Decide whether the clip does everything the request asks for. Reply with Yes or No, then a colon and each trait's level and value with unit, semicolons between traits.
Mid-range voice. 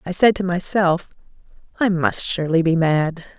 Yes: medium, 175 Hz